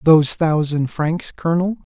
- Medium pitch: Yes, medium, 160 Hz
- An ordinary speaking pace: No, slow, 125 wpm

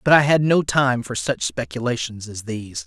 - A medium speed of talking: No, fast, 210 wpm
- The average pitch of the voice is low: Yes, low, 120 Hz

